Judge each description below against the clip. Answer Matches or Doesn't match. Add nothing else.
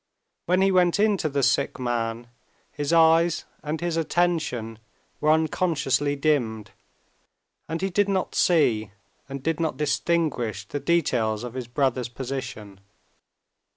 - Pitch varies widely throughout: Matches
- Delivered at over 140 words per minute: Doesn't match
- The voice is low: Doesn't match